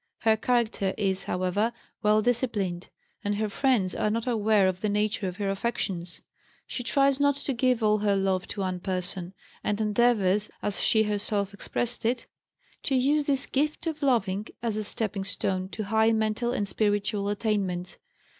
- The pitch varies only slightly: No, average, 3.3 semitones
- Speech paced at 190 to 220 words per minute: No, average, 170 wpm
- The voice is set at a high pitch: Yes, high, 210 Hz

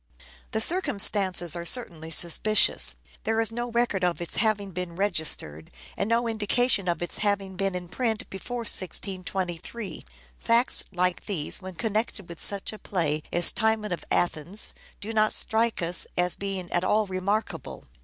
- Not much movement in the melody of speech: No, average, 3.8 semitones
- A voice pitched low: No, high, 195 Hz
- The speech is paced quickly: No, average, 160 wpm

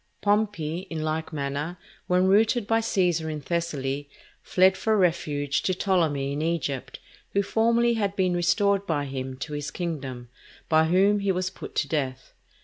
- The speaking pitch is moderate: Yes, medium, 170 Hz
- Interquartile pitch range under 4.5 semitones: No, average, 5.3 semitones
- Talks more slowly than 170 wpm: Yes, average, 160 wpm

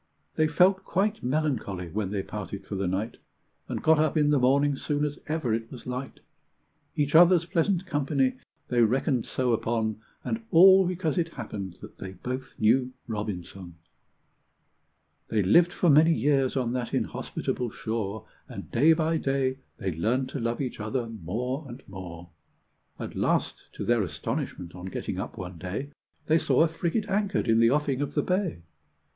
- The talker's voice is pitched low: Yes, low, 130 Hz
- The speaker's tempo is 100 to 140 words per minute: No, average, 170 wpm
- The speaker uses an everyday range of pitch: No, wide, 6.5 semitones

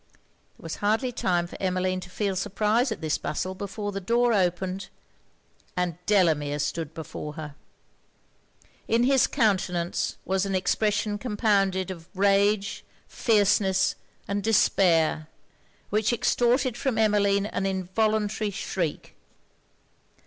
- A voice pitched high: Yes, high, 195 Hz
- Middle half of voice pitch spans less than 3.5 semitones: Yes, average, 2.9 semitones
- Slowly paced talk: Yes, slow, 120 wpm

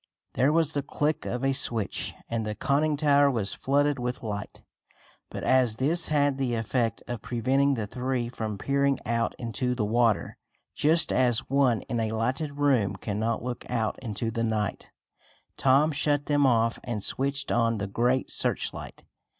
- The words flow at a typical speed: Yes, average, 165 wpm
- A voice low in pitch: Yes, low, 125 Hz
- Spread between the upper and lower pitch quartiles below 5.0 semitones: Yes, average, 3.6 semitones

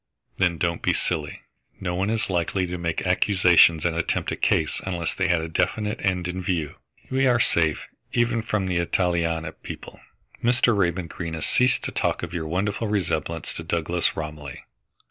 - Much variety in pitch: No, average, 2.9 semitones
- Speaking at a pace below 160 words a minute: No, average, 180 wpm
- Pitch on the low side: Yes, very low, 90 Hz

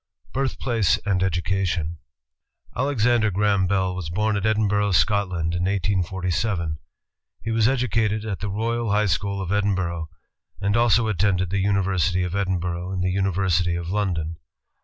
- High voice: No, very low, 95 Hz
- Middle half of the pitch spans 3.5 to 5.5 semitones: No, average, 2.7 semitones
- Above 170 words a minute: No, average, 150 wpm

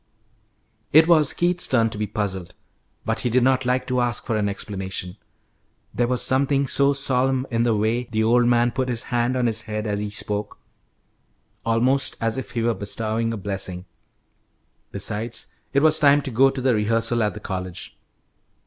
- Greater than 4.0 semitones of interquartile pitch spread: No, average, 3.3 semitones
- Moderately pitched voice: No, low, 115 Hz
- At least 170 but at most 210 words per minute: Yes, average, 185 wpm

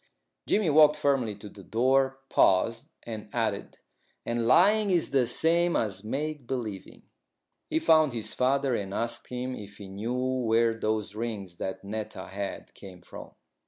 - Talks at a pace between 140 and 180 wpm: Yes, average, 155 wpm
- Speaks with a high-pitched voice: No, low, 115 Hz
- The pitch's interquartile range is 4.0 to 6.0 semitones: Yes, average, 4.6 semitones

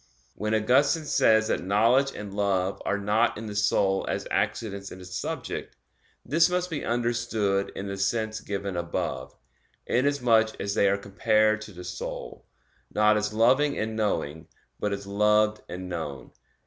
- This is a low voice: Yes, low, 105 Hz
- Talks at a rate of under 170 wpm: Yes, average, 160 wpm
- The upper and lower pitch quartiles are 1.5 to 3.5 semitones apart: Yes, narrow, 2.5 semitones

